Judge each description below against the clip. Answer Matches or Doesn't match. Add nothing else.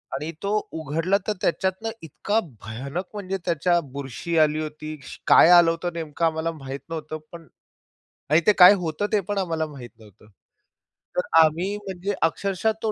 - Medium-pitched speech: Matches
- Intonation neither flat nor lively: Matches